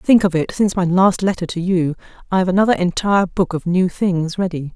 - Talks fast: Yes, fast, 225 wpm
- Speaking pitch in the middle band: Yes, medium, 180 Hz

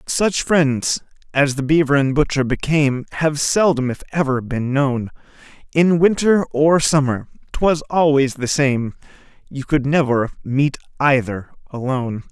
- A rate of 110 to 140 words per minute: Yes, slow, 135 wpm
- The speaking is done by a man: Yes, male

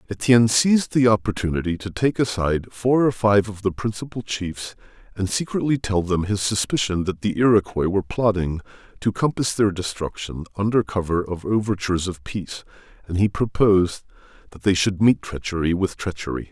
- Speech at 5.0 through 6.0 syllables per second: Yes, 5.5 syllables/s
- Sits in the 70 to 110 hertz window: Yes, low, 100 Hz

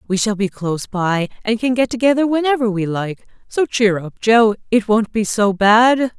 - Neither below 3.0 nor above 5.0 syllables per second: Yes, 4.8 syllables/s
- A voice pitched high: Yes, high, 220 Hz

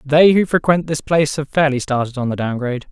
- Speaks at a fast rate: Yes, fast, 245 wpm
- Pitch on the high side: No, medium, 145 Hz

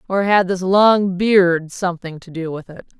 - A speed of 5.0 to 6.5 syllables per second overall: No, 4.4 syllables/s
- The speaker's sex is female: Yes, female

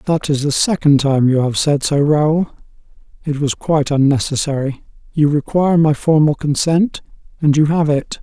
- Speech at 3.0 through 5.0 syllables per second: Yes, 4.9 syllables/s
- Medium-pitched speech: Yes, medium, 150 Hz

